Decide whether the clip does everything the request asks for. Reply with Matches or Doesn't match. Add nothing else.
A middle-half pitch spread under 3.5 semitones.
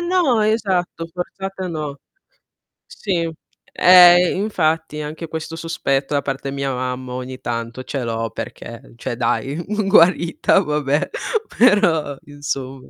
Doesn't match